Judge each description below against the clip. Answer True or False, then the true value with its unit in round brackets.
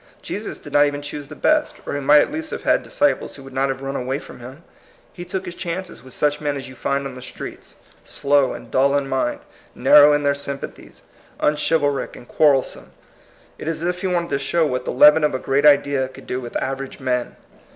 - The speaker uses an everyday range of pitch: False (2.2 semitones)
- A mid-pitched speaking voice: True (145 Hz)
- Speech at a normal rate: False (235 wpm)